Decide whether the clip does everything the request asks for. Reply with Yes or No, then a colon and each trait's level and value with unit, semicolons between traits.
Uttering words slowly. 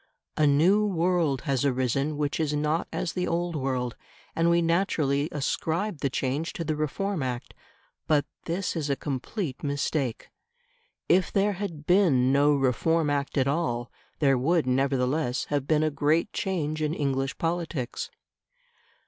No: average, 150 wpm